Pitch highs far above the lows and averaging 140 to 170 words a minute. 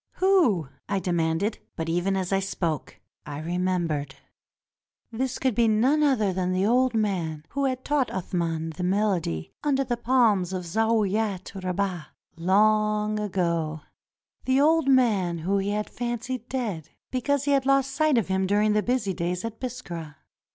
Yes: wide, 5.8 semitones; average, 165 wpm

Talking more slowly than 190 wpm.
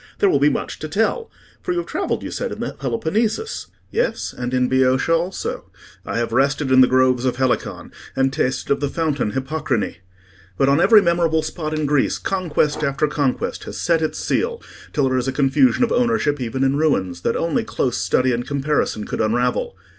No: average, 200 wpm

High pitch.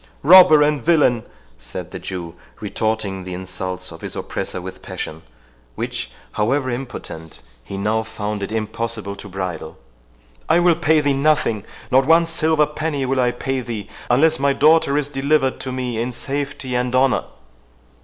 No: low, 125 Hz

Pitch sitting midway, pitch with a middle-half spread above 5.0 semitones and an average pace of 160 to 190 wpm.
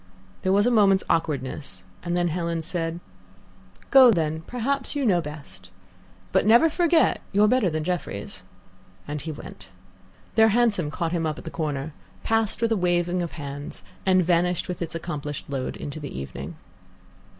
Yes: medium, 175 Hz; wide, 5.5 semitones; average, 165 wpm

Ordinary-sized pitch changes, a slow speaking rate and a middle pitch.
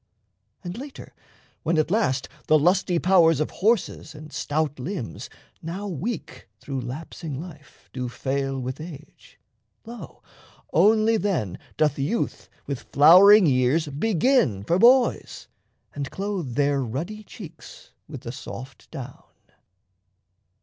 No: wide, 6.3 semitones; slow, 120 wpm; medium, 160 Hz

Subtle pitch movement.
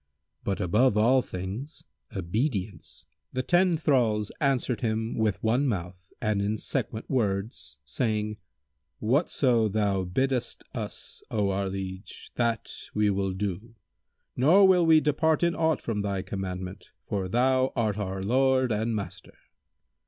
No: average, 4.9 semitones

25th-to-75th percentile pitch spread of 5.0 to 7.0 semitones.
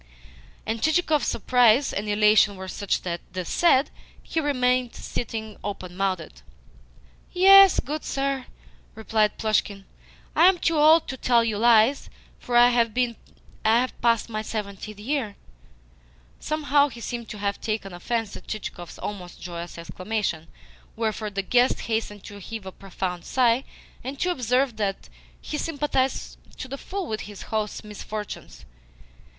No: average, 4.4 semitones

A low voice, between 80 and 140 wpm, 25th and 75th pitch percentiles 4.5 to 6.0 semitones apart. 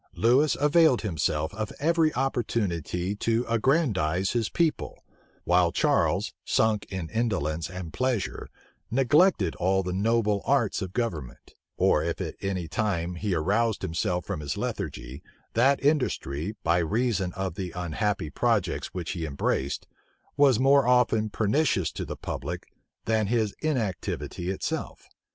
Yes: low, 105 Hz; slow, 135 wpm; wide, 5.5 semitones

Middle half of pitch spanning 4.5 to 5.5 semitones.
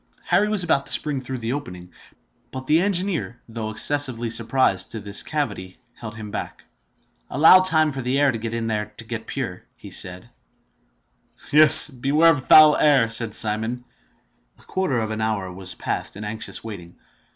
Yes: average, 5.2 semitones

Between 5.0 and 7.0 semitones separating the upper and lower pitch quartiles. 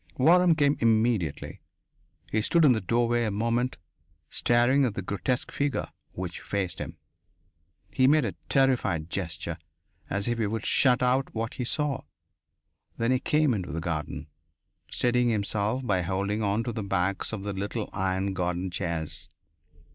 No: average, 4.6 semitones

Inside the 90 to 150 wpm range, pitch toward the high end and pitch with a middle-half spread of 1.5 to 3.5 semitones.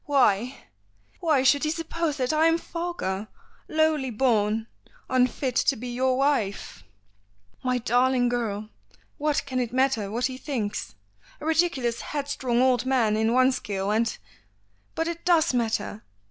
No: average, 145 wpm; very high, 255 Hz; average, 4.4 semitones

